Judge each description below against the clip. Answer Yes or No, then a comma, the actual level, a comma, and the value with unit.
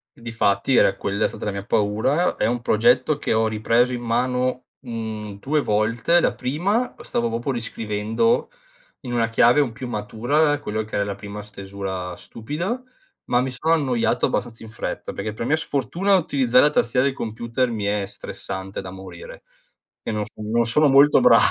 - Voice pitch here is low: Yes, low, 115 Hz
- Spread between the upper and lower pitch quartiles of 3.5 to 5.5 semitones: Yes, average, 4.5 semitones